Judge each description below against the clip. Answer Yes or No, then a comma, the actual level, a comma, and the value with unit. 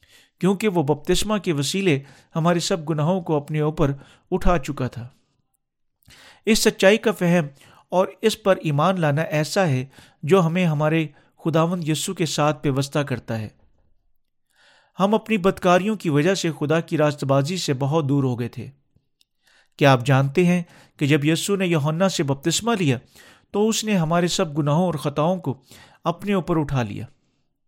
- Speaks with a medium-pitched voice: Yes, medium, 160 Hz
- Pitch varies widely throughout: No, average, 4.8 semitones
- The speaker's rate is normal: Yes, average, 165 wpm